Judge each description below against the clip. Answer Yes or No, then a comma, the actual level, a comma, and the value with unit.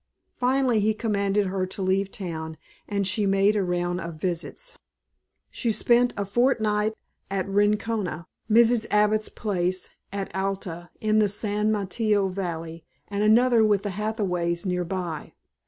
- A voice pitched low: No, high, 200 Hz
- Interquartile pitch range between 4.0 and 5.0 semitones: No, average, 2.7 semitones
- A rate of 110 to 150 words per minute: Yes, average, 140 wpm